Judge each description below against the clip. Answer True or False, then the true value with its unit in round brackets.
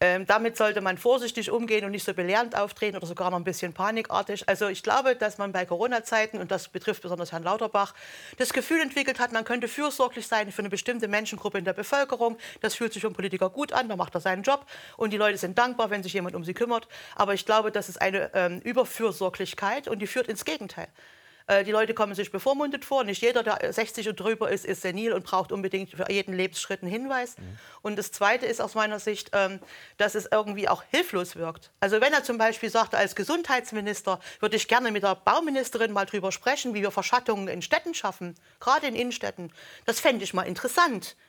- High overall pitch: True (210 Hz)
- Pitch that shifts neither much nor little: True (3.5 semitones)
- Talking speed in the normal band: False (215 wpm)